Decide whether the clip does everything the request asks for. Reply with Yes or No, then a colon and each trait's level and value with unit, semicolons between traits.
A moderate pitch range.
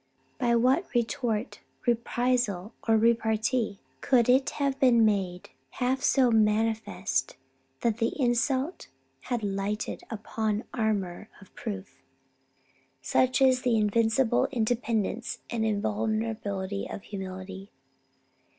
Yes: average, 3.4 semitones